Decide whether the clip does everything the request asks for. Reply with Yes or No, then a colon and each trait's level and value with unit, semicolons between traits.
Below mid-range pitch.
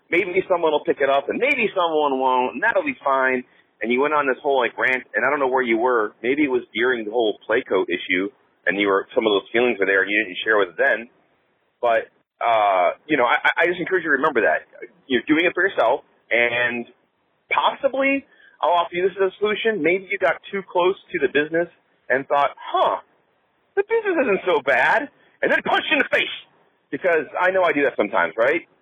No: medium, 175 Hz